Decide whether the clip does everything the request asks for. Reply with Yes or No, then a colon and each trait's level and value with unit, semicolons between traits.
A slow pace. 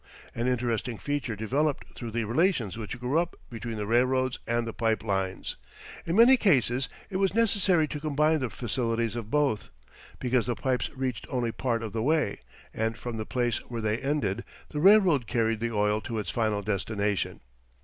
No: average, 180 wpm